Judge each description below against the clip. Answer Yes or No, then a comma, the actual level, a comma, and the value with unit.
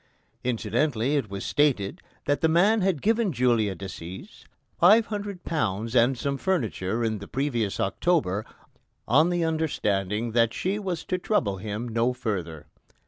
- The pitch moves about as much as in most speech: No, wide, 8.2 semitones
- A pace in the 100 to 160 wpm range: Yes, average, 140 wpm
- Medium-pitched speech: No, low, 125 Hz